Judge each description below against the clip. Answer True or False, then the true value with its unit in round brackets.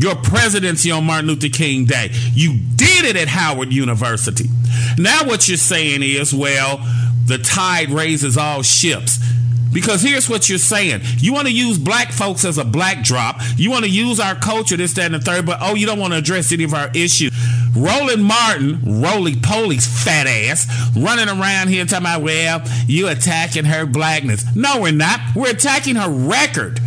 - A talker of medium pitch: True (150 Hz)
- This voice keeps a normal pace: True (190 wpm)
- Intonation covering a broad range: True (6.7 semitones)